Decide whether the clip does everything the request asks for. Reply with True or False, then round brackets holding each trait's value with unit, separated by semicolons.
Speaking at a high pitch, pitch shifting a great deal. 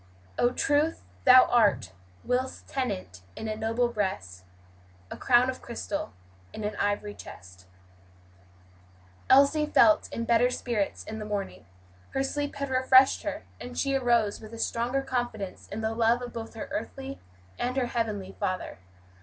False (235 Hz; 3.7 semitones)